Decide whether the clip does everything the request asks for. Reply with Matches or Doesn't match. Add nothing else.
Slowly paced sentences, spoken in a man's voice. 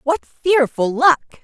Doesn't match